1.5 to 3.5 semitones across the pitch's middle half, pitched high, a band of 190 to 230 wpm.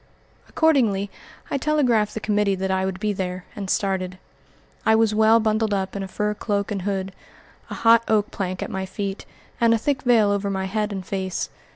Yes: narrow, 2.4 semitones; high, 205 Hz; average, 200 wpm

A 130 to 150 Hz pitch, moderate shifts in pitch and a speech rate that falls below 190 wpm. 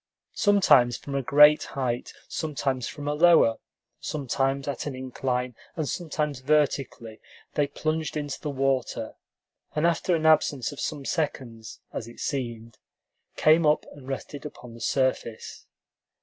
Yes: medium, 140 Hz; average, 3.1 semitones; average, 140 wpm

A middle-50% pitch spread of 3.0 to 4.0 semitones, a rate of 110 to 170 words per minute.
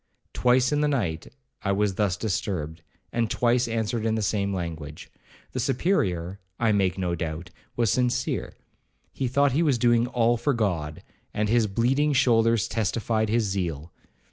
No: average, 4.6 semitones; average, 160 wpm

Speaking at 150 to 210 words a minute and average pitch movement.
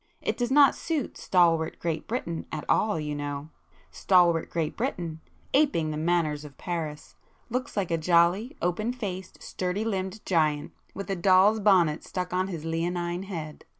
Yes: average, 155 wpm; average, 3.6 semitones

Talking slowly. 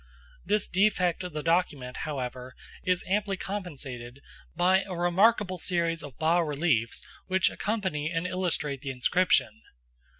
Yes: slow, 130 wpm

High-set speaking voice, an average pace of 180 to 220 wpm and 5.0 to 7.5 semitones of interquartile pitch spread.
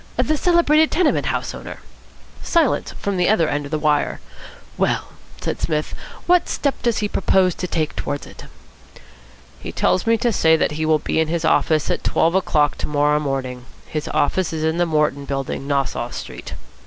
No: medium, 160 Hz; average, 185 wpm; average, 5.3 semitones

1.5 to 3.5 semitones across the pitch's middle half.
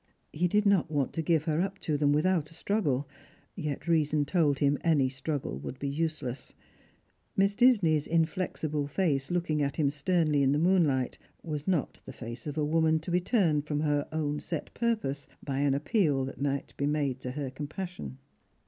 Yes: average, 3.1 semitones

